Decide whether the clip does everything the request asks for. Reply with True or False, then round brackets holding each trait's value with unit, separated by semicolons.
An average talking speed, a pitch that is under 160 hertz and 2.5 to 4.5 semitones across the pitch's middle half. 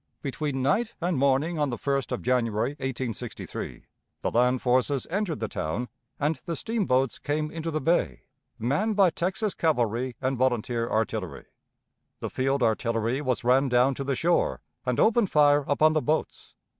True (160 wpm; 135 Hz; 4.1 semitones)